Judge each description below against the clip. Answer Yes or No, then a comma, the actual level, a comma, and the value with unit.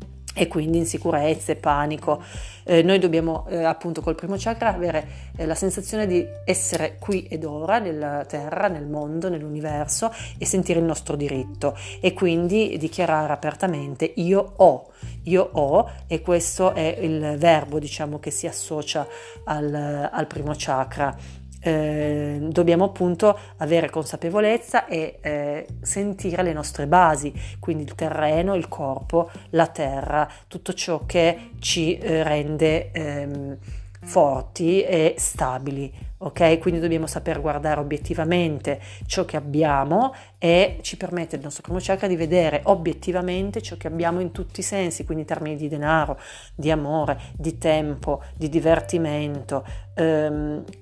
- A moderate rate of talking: Yes, average, 140 wpm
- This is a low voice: No, medium, 160 Hz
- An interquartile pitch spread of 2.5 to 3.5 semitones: Yes, average, 2.8 semitones